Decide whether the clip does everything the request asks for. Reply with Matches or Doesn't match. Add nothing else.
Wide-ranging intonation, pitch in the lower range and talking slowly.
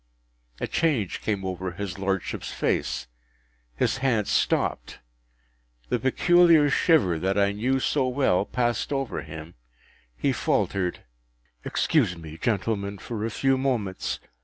Matches